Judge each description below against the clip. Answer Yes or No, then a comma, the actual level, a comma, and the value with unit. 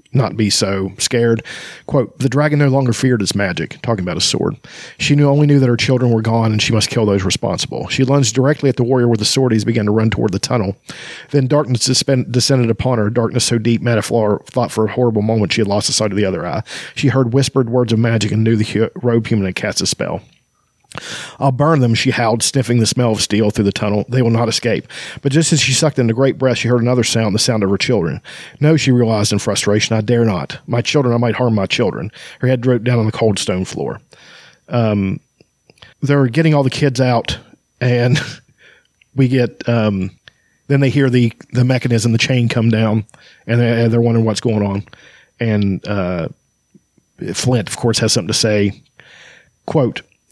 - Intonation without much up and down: No, average, 3.2 semitones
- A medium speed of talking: No, fast, 220 wpm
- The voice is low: Yes, low, 120 Hz